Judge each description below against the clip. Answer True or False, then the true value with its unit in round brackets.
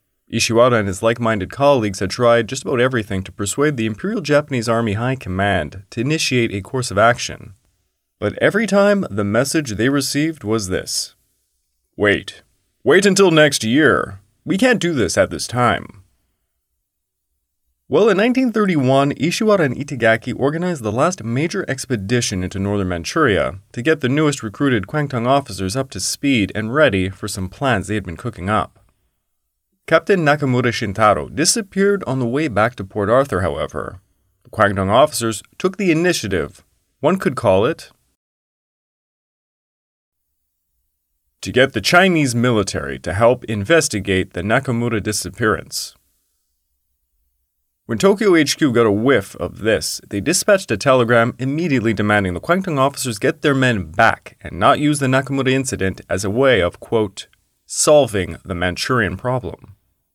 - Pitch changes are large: True (6.6 semitones)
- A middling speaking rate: True (150 wpm)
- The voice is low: True (115 Hz)